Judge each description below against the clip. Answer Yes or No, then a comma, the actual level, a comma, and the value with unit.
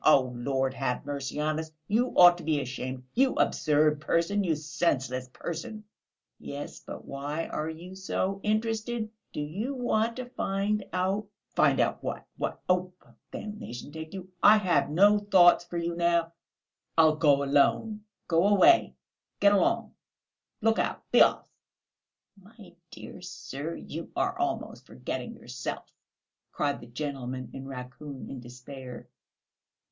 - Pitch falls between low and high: Yes, medium, 165 Hz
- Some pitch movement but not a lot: No, wide, 6.3 semitones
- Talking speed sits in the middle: Yes, average, 145 wpm